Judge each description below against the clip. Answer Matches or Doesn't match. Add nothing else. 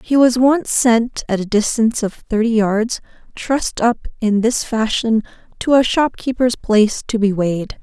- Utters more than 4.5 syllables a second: Doesn't match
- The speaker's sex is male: Doesn't match